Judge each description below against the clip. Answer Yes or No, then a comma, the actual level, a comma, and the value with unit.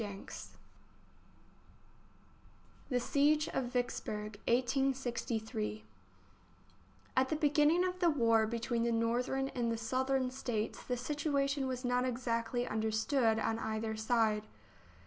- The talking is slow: Yes, slow, 125 wpm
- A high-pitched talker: Yes, high, 245 Hz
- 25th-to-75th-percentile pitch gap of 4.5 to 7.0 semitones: No, average, 3.1 semitones